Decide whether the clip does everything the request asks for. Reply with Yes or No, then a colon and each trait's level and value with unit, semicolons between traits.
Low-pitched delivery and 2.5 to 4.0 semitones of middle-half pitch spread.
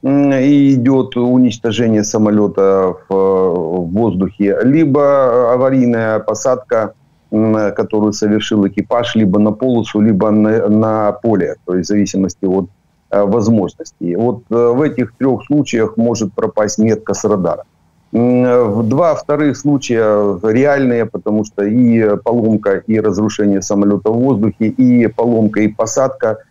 Yes: low, 110 Hz; average, 2.8 semitones